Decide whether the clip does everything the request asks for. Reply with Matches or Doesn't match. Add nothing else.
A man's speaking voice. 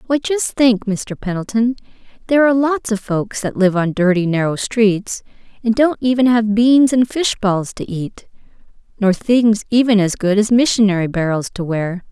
Doesn't match